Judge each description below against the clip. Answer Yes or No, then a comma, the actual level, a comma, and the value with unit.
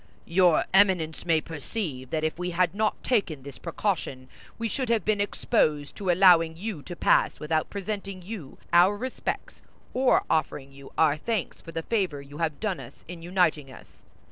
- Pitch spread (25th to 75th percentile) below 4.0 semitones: No, average, 4.6 semitones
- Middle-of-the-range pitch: Yes, medium, 175 Hz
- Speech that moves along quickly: No, average, 175 wpm